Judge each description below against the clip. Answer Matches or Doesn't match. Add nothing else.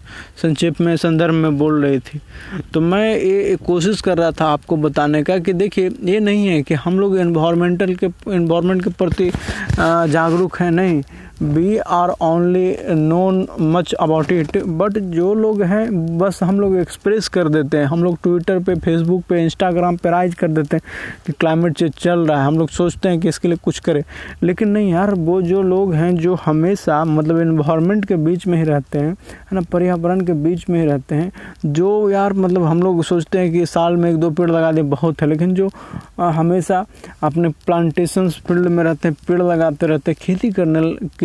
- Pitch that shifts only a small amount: Matches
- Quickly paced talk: Matches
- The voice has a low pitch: Doesn't match